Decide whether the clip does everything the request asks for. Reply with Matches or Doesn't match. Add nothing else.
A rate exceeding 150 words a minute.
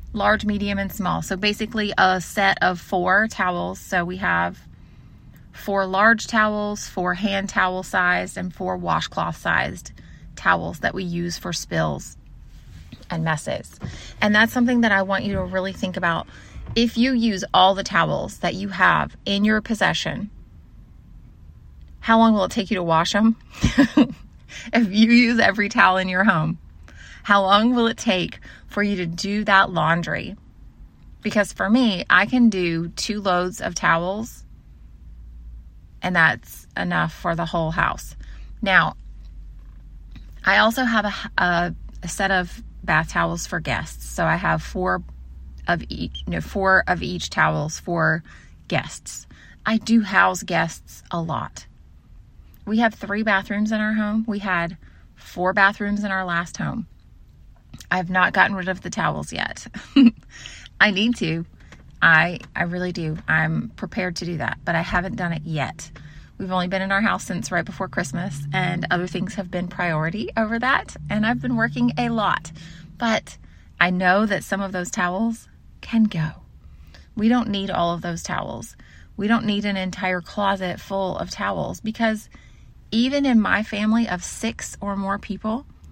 Matches